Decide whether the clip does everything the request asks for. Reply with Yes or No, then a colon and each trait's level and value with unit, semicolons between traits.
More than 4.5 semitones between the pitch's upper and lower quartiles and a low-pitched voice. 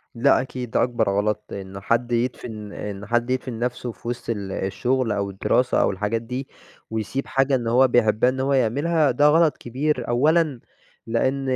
No: average, 3.2 semitones; low, 120 Hz